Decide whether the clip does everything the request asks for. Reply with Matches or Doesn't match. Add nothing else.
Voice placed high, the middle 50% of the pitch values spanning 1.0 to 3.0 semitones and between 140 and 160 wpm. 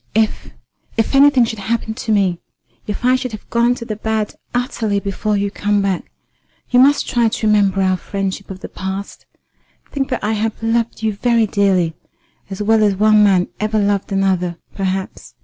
Doesn't match